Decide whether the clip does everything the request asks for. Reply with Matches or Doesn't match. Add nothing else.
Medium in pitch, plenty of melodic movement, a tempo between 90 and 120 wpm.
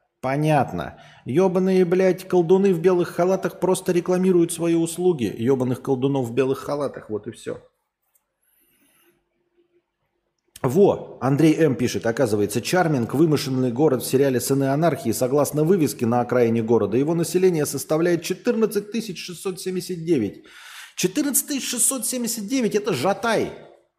Matches